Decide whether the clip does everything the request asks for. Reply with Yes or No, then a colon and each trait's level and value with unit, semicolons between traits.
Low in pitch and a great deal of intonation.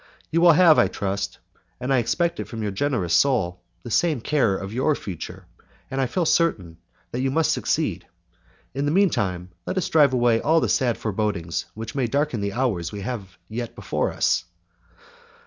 Yes: low, 120 Hz; wide, 6.7 semitones